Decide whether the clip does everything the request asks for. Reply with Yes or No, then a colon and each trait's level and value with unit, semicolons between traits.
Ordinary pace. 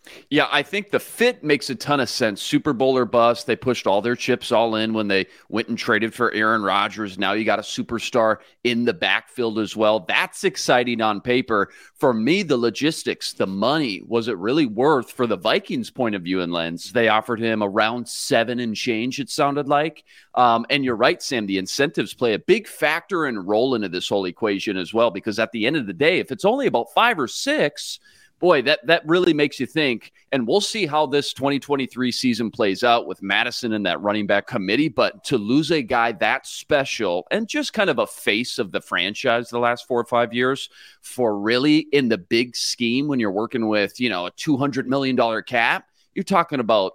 No: fast, 215 wpm